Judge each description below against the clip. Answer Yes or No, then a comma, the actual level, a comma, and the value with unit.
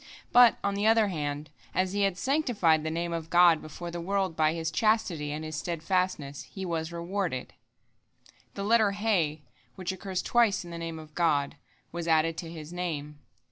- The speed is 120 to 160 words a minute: No, average, 180 wpm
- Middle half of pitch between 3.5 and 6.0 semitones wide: Yes, average, 3.8 semitones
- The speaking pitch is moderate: Yes, medium, 170 Hz